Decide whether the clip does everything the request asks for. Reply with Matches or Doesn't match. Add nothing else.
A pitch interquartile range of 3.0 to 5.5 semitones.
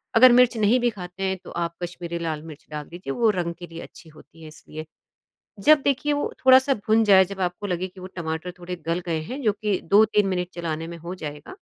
Matches